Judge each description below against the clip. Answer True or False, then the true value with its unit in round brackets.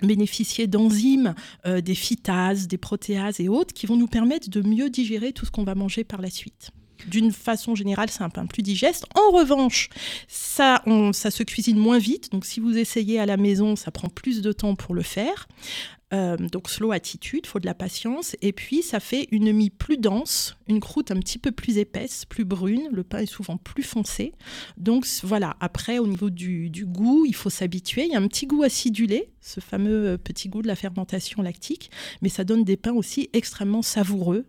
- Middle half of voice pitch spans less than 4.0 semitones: True (3.2 semitones)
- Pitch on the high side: True (215 Hz)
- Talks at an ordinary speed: True (210 wpm)